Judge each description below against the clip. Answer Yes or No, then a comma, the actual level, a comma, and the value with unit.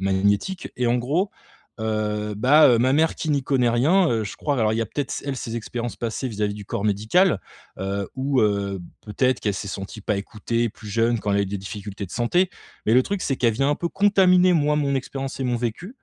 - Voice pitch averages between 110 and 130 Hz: Yes, low, 120 Hz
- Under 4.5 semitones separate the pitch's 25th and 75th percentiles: No, average, 5.1 semitones